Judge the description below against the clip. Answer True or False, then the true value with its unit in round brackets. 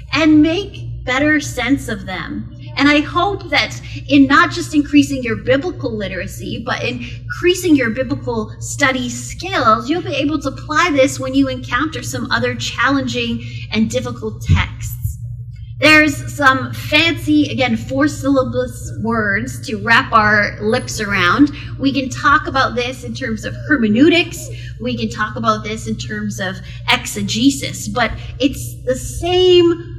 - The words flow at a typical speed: True (145 wpm)